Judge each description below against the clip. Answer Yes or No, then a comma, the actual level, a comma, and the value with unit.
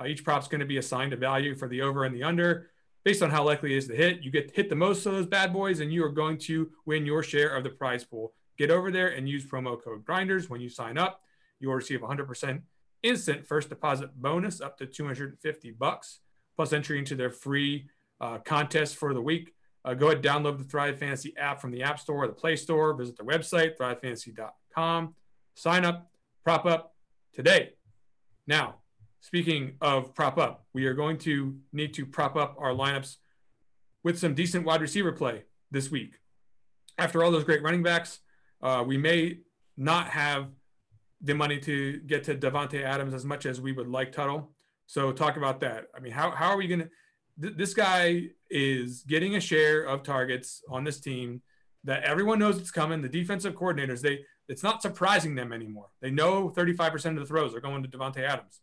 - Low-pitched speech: No, medium, 150 Hz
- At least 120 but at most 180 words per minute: No, fast, 205 wpm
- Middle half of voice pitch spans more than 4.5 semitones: No, average, 3.5 semitones